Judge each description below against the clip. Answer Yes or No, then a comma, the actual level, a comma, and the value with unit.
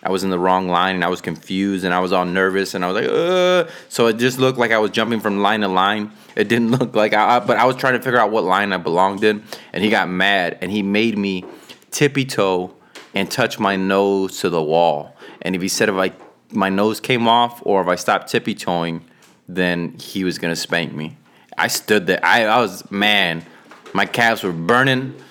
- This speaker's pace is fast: Yes, fast, 235 wpm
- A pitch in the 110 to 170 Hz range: No, low, 100 Hz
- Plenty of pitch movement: No, average, 3.9 semitones